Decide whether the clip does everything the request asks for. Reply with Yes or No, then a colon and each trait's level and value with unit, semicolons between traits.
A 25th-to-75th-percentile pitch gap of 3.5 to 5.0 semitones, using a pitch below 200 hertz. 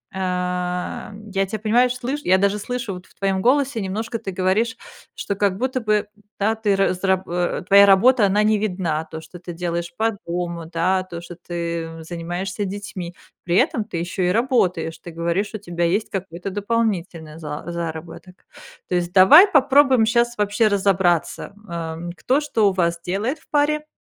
Yes: average, 4.0 semitones; high, 190 Hz